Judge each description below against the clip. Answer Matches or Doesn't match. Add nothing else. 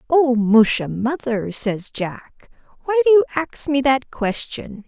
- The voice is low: Doesn't match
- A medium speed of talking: Matches